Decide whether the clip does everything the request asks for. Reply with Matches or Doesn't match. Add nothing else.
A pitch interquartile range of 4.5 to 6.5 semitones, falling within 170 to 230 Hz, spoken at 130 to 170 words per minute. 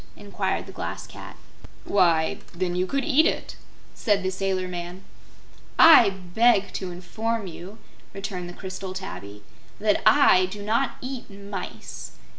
Doesn't match